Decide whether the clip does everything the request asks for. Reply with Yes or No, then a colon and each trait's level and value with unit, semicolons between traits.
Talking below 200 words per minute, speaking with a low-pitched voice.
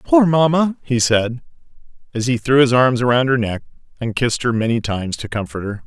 No: fast, 205 wpm; low, 125 Hz